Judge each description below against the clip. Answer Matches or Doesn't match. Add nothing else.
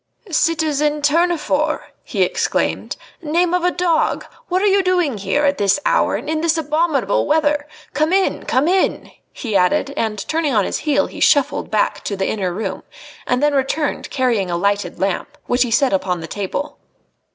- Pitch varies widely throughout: Matches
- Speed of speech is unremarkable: Matches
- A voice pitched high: Matches